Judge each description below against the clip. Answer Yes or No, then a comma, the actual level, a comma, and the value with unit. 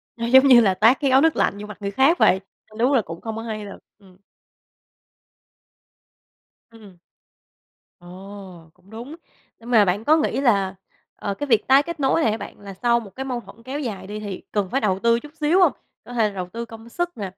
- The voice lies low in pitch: No, high, 225 Hz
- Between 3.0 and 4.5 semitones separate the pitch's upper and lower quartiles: No, average, 4.9 semitones